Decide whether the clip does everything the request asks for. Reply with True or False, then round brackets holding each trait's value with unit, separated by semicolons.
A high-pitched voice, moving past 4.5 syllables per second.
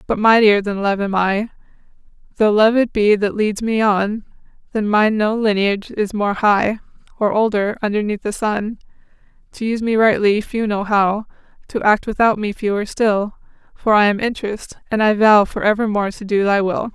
True (210 Hz; 5.0 syllables/s)